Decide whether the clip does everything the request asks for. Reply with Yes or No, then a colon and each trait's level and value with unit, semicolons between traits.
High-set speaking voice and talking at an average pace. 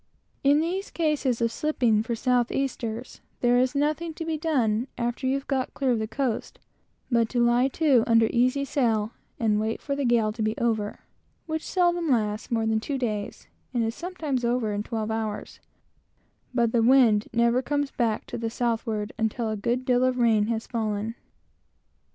Yes: high, 240 Hz; average, 190 wpm